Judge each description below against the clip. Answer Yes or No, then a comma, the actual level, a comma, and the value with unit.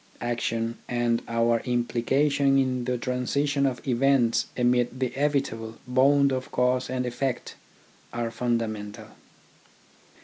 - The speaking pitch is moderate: No, low, 125 Hz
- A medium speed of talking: No, slow, 110 wpm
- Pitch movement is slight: Yes, narrow, 2.3 semitones